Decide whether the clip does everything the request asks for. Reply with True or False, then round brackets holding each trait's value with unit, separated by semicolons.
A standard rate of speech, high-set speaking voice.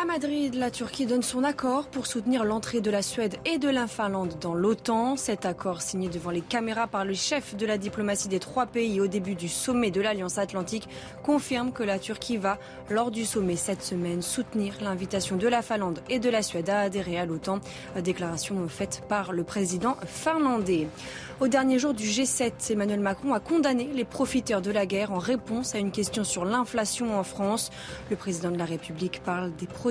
True (205 wpm; 210 Hz)